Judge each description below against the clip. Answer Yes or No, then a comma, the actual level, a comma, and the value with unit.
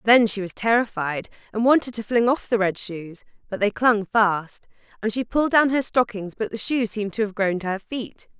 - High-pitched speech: Yes, high, 215 Hz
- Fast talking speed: Yes, fast, 230 wpm